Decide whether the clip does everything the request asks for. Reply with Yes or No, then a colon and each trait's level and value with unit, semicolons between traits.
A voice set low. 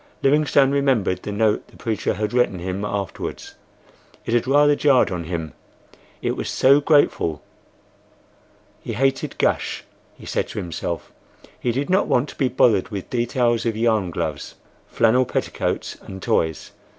Yes: low, 115 Hz